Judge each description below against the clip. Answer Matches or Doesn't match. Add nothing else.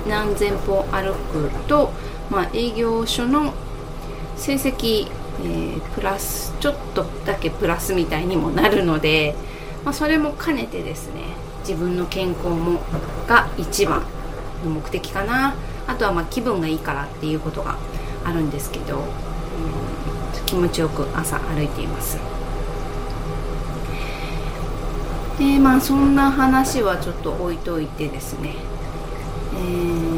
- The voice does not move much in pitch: Doesn't match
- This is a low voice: Doesn't match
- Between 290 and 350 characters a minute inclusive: Doesn't match